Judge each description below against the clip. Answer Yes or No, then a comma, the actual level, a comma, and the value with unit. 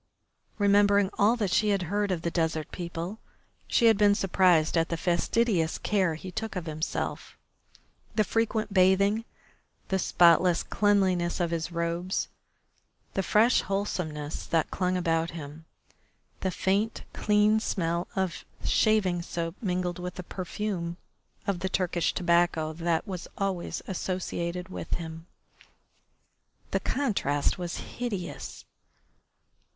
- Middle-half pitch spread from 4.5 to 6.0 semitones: No, average, 3.1 semitones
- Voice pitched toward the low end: No, medium, 180 Hz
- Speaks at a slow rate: Yes, slow, 125 wpm